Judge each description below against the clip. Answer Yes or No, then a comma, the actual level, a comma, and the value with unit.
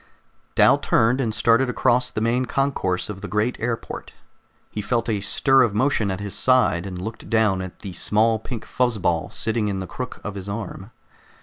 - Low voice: Yes, low, 110 Hz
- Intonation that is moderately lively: Yes, average, 3.5 semitones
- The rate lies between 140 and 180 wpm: No, average, 195 wpm